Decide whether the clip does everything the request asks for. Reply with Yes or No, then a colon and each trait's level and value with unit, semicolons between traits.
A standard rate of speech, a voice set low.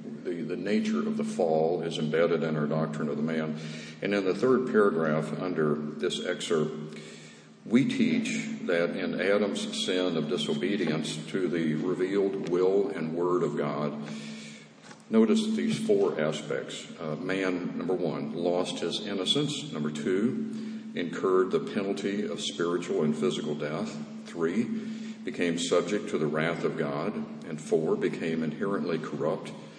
Yes: average, 145 wpm; very low, 95 Hz